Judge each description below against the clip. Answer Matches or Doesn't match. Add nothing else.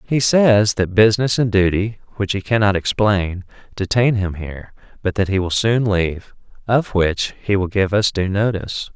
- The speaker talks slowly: Doesn't match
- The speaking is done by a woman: Doesn't match